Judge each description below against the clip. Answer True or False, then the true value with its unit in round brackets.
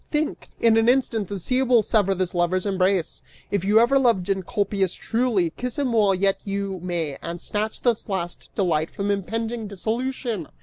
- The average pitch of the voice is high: True (200 Hz)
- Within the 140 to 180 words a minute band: True (175 wpm)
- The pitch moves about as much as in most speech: True (3.8 semitones)